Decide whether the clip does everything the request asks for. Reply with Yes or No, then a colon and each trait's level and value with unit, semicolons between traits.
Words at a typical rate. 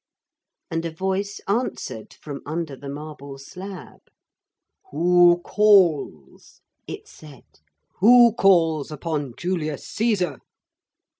No: slow, 95 wpm